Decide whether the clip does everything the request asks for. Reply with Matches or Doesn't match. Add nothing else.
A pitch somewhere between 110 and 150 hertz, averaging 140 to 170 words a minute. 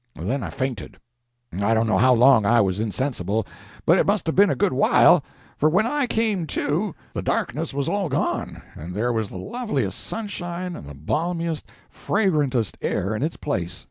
Doesn't match